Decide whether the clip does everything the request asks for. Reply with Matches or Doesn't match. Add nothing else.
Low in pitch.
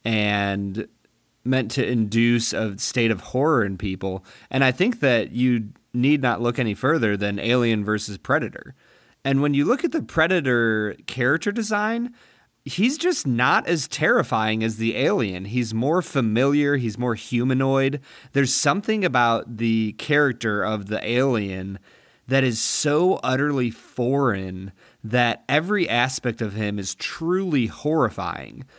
Matches